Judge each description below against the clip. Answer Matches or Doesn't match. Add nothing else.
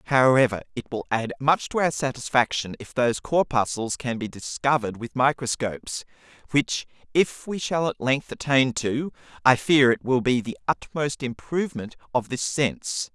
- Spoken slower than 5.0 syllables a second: Matches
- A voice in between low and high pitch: Doesn't match